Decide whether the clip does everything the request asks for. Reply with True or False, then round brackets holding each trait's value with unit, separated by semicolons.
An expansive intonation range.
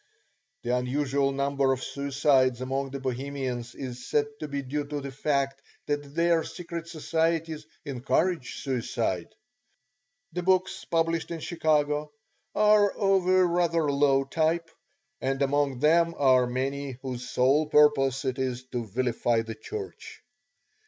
False (3.8 semitones)